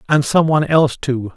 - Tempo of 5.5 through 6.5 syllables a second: Yes, 6.0 syllables/s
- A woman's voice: No, male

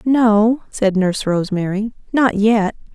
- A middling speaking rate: No, slow, 120 wpm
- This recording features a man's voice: No, female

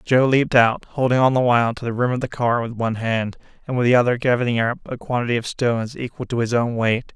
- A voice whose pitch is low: Yes, low, 120 Hz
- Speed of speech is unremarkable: No, fast, 260 wpm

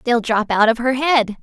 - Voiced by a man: No, female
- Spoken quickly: Yes, fast, 250 wpm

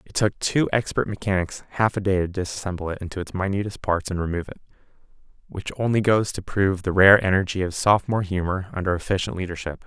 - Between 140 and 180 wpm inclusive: No, average, 195 wpm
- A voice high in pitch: No, very low, 95 Hz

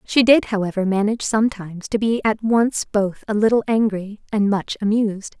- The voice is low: No, high, 210 Hz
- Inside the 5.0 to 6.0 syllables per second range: Yes, 5.4 syllables/s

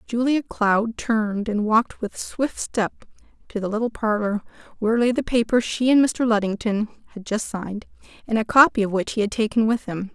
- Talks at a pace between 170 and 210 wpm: Yes, average, 195 wpm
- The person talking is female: Yes, female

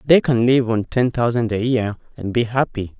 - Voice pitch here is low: Yes, low, 120 Hz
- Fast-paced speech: Yes, fast, 220 wpm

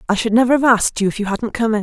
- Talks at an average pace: No, fast, 360 wpm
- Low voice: No, high, 220 Hz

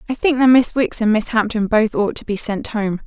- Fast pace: Yes, fast, 275 wpm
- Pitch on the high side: Yes, high, 225 Hz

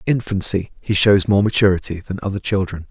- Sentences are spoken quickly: No, average, 185 wpm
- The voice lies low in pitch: Yes, low, 100 Hz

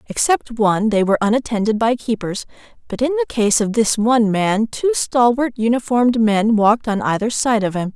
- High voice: Yes, high, 225 Hz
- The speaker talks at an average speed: Yes, average, 190 wpm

